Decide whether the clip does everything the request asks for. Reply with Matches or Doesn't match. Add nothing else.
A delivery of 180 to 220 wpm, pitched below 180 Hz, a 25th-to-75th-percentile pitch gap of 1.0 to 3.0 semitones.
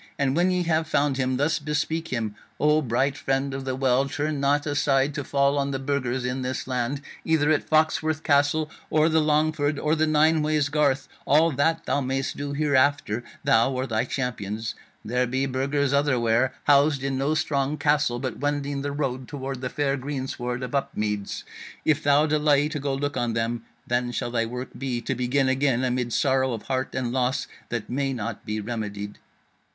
Matches